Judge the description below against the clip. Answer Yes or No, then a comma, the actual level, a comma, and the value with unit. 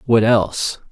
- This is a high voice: No, low, 110 Hz